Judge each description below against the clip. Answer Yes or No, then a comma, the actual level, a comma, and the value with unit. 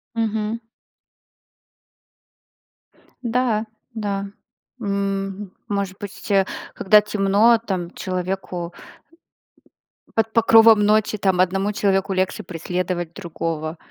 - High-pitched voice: Yes, high, 195 Hz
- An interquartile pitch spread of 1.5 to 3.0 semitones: Yes, narrow, 2.5 semitones